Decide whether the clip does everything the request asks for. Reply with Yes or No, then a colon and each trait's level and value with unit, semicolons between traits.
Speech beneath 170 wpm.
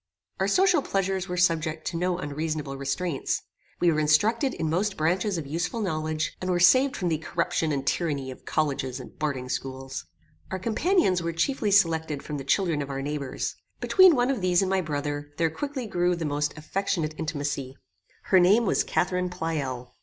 No: average, 185 wpm